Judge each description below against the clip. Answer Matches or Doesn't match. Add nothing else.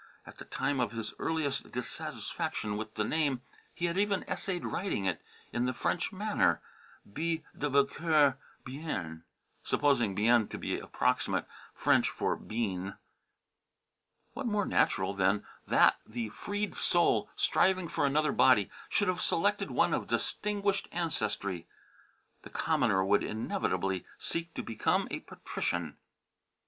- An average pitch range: Doesn't match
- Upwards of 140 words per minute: Doesn't match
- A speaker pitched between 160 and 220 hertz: Doesn't match